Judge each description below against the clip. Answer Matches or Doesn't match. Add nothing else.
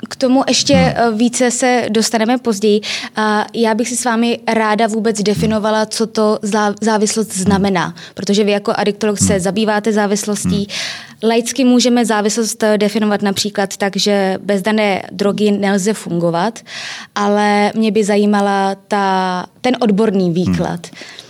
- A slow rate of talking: Doesn't match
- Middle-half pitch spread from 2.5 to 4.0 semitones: Doesn't match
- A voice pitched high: Matches